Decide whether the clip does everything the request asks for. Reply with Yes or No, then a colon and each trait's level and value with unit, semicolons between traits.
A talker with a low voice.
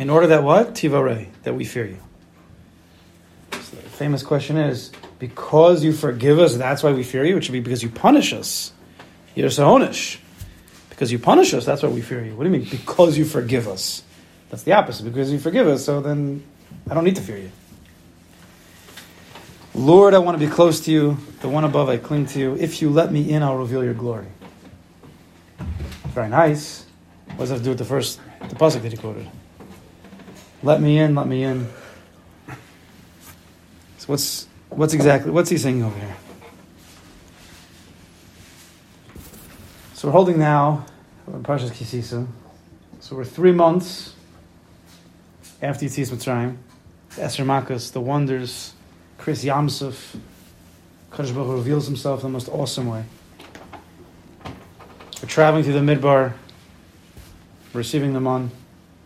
Yes: low, 125 Hz